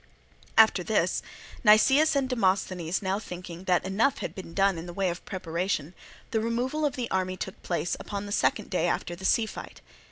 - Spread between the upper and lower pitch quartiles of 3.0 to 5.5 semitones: Yes, average, 4.2 semitones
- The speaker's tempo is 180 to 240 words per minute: Yes, average, 190 wpm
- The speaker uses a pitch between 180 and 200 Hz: Yes, high, 190 Hz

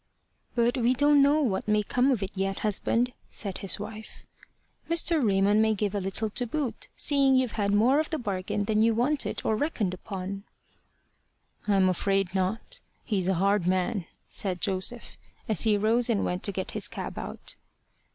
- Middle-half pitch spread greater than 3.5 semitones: Yes, average, 4.0 semitones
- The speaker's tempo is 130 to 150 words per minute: No, average, 180 wpm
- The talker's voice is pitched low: No, high, 210 Hz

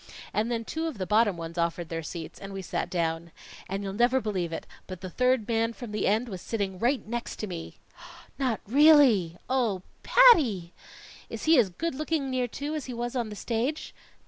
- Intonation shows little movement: No, wide, 5.5 semitones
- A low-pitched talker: No, high, 225 Hz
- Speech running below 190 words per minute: No, fast, 205 wpm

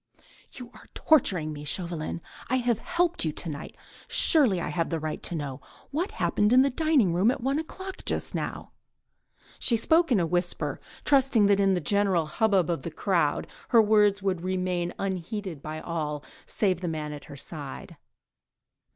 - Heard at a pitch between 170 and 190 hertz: Yes, medium, 185 Hz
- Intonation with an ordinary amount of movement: No, wide, 6.4 semitones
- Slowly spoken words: No, average, 175 wpm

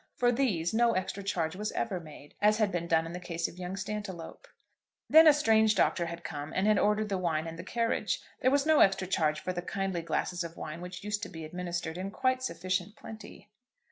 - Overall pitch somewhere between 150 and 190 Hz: Yes, medium, 185 Hz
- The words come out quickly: Yes, fast, 225 wpm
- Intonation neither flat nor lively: Yes, average, 3.9 semitones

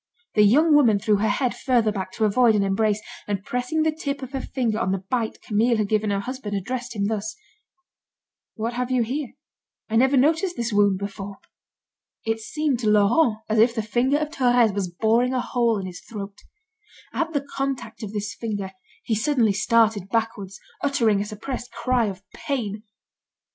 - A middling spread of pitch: Yes, average, 3.6 semitones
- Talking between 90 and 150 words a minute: No, average, 185 wpm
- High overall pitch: Yes, high, 225 Hz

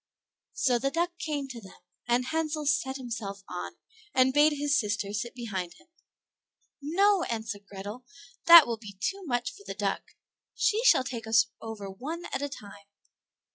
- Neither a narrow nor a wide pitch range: No, wide, 6.0 semitones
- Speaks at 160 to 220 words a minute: Yes, average, 170 wpm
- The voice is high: Yes, very high, 250 Hz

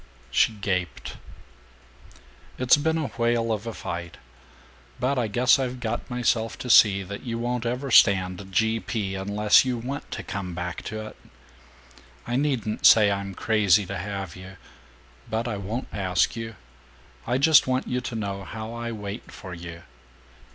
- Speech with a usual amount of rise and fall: Yes, average, 3.7 semitones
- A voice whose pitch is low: Yes, low, 110 Hz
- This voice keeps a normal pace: Yes, average, 165 wpm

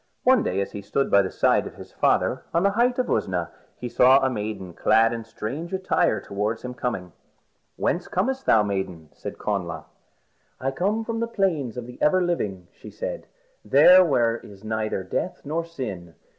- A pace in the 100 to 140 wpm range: No, average, 190 wpm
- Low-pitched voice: Yes, low, 125 Hz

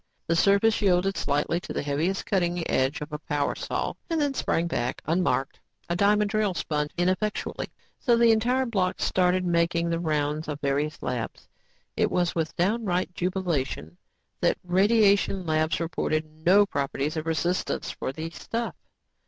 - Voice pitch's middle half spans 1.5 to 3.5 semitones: No, average, 4.3 semitones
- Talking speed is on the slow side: No, average, 160 wpm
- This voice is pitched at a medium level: Yes, medium, 175 Hz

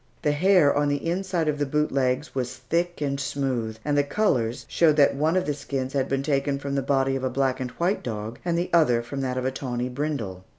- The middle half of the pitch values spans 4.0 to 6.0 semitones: No, average, 2.8 semitones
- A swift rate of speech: Yes, fast, 245 wpm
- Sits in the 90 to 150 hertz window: Yes, medium, 140 Hz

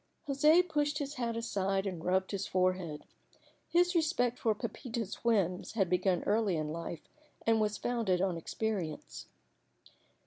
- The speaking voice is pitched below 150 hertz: No, high, 210 Hz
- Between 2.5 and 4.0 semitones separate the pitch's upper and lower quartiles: No, average, 5.0 semitones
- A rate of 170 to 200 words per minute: No, average, 140 wpm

